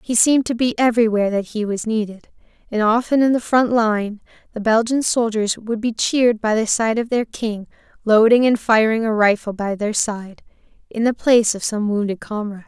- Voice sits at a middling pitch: No, high, 220 Hz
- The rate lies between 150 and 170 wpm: No, average, 200 wpm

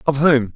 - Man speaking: Yes, male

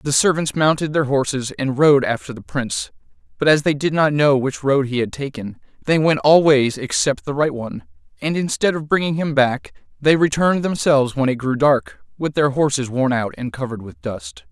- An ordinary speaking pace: No, fast, 210 wpm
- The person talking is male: Yes, male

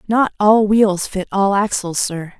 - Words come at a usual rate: Yes, average, 175 wpm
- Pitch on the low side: No, high, 200 Hz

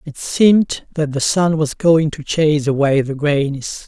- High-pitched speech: No, medium, 150 Hz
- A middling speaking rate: Yes, average, 185 wpm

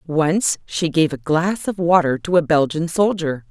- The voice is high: No, medium, 165 Hz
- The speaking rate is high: No, average, 190 wpm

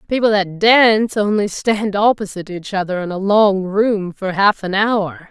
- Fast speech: No, average, 180 wpm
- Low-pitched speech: No, high, 200 Hz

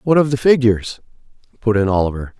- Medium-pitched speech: No, low, 115 Hz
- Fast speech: No, average, 175 wpm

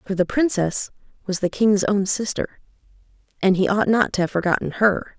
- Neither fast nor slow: Yes, average, 185 wpm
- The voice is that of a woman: Yes, female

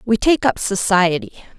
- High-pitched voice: Yes, high, 210 Hz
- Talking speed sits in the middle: Yes, average, 150 wpm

